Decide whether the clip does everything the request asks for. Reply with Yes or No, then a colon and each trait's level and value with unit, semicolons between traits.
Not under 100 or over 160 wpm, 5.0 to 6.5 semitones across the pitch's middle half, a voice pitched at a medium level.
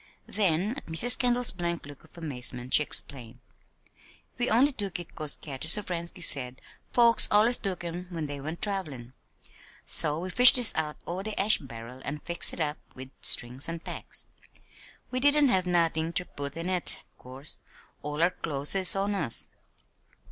No: average, 170 wpm; wide, 5.4 semitones; medium, 170 Hz